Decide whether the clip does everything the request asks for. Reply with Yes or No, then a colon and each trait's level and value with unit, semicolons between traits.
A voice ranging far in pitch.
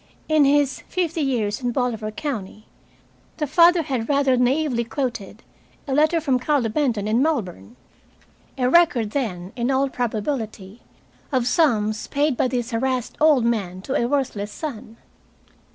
No: average, 4.6 semitones